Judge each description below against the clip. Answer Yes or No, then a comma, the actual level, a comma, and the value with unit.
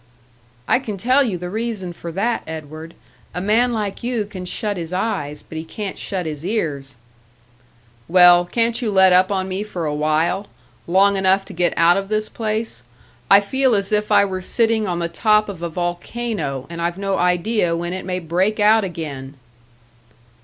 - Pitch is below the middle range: No, medium, 185 Hz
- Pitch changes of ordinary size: Yes, average, 3.9 semitones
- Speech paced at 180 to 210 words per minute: Yes, average, 185 wpm